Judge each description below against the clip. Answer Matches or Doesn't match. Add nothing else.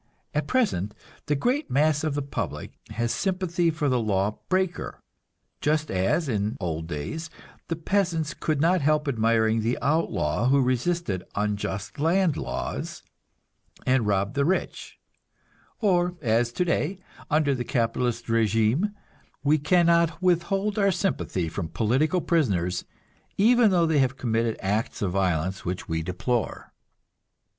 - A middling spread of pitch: Doesn't match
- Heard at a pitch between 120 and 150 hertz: Matches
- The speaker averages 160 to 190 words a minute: Doesn't match